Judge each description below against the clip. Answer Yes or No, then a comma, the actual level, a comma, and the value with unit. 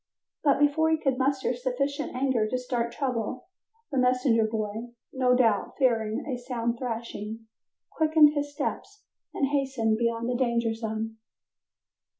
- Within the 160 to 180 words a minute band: No, average, 140 wpm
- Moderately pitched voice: No, very high, 250 Hz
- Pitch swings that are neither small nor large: Yes, average, 3.2 semitones